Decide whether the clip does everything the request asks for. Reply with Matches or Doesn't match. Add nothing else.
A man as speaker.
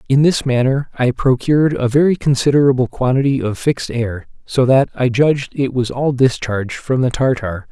Matches